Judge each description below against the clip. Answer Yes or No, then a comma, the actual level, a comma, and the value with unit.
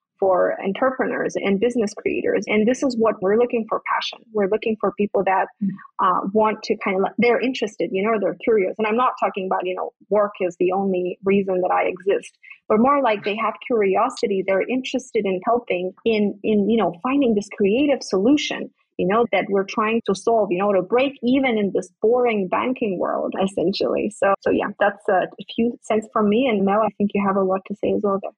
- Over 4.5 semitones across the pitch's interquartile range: No, average, 3.5 semitones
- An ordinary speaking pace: No, fast, 220 wpm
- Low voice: No, high, 215 Hz